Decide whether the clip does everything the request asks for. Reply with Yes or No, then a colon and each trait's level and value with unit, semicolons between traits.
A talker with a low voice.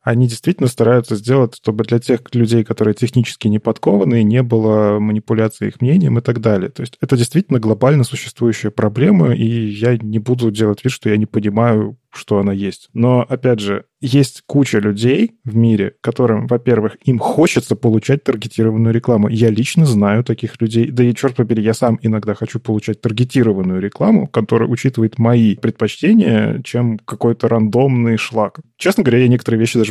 Yes: low, 115 Hz